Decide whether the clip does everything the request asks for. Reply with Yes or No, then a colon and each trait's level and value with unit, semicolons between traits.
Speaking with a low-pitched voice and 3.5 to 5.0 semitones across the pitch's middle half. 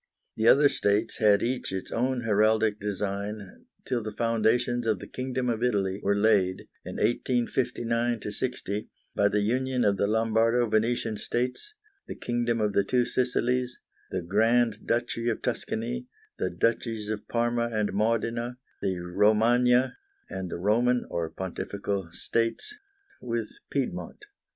No: low, 115 Hz; average, 2.9 semitones